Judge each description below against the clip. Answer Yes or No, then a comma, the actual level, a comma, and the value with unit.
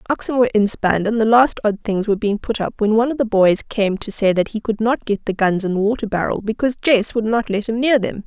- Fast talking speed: Yes, fast, 285 wpm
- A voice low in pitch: No, high, 220 Hz